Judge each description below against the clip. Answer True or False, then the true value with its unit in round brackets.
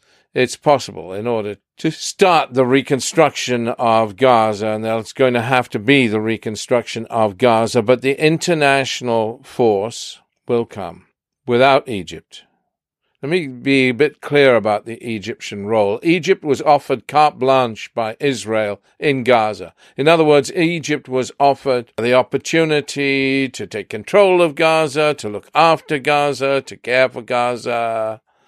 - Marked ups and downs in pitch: False (4.1 semitones)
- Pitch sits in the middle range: False (130 Hz)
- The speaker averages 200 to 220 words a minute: False (145 wpm)